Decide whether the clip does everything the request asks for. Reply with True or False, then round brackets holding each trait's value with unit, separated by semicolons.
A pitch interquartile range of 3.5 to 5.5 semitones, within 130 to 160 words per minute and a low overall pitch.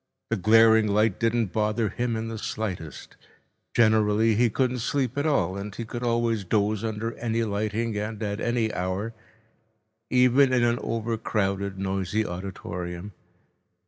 False (2.4 semitones; 145 wpm; 110 Hz)